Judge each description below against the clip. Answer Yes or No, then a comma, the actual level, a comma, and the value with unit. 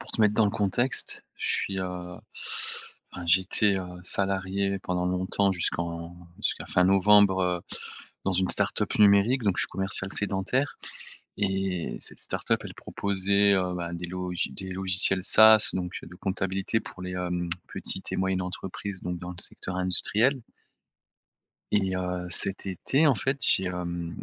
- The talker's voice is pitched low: Yes, very low, 95 Hz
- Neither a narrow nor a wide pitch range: No, narrow, 1.8 semitones